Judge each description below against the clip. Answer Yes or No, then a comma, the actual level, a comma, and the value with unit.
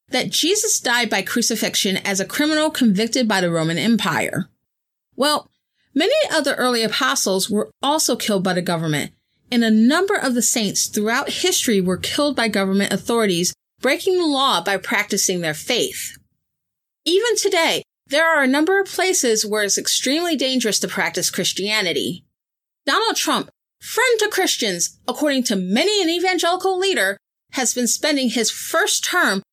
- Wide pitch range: Yes, wide, 7.6 semitones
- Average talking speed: Yes, average, 155 wpm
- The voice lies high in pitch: Yes, high, 240 Hz